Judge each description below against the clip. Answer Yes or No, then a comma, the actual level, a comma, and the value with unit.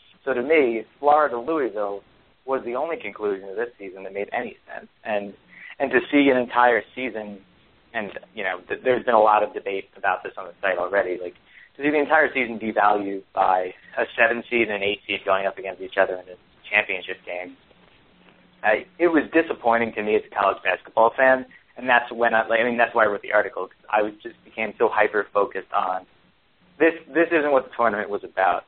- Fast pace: Yes, fast, 215 wpm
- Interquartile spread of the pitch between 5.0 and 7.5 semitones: No, average, 4.6 semitones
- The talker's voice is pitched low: Yes, low, 115 Hz